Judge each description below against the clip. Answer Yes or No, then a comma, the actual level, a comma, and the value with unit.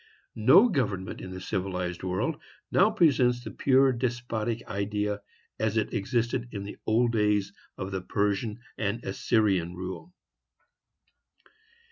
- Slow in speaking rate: Yes, slow, 125 wpm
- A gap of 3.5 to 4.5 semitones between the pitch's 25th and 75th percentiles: Yes, average, 3.9 semitones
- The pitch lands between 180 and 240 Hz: No, low, 105 Hz